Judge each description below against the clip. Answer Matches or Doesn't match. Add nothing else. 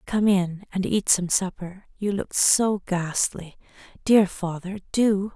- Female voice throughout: Matches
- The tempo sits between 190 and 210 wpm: Doesn't match